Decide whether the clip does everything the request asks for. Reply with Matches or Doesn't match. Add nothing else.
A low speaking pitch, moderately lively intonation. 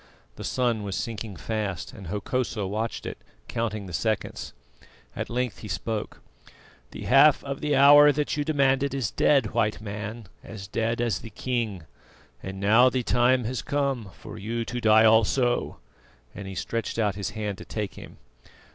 Matches